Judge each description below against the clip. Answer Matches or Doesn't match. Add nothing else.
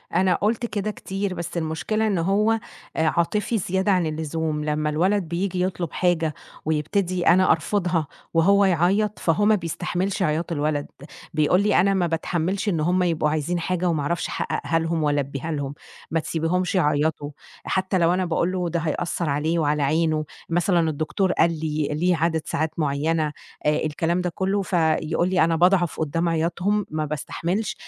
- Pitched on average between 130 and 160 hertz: Doesn't match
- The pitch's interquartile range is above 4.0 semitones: Doesn't match